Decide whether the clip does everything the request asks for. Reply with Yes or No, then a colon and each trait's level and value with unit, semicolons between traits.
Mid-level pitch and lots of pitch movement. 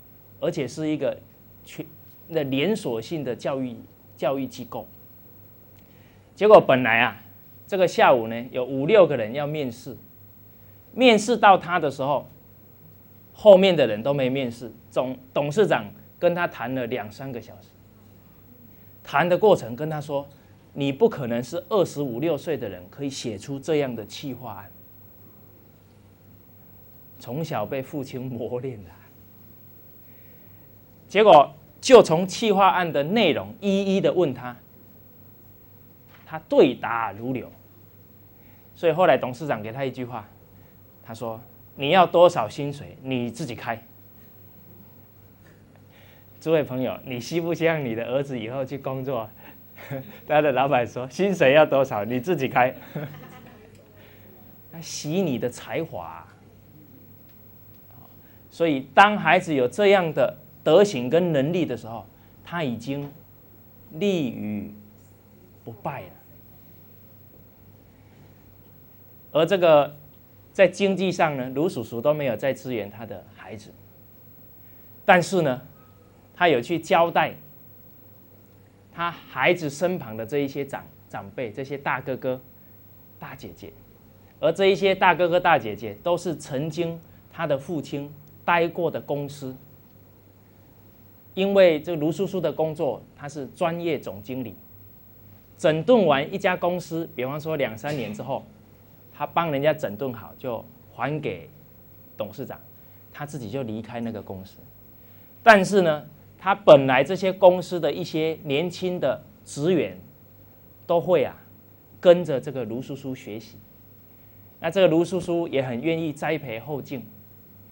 No: low, 120 Hz; wide, 6.5 semitones